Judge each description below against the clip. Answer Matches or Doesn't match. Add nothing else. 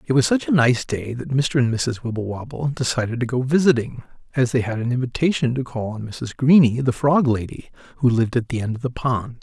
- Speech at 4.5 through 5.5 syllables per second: Doesn't match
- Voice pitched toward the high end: Doesn't match